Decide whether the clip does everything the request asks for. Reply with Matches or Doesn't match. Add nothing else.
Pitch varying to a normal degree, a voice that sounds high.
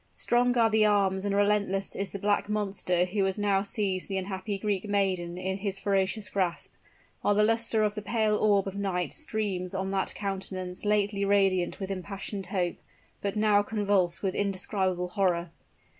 Doesn't match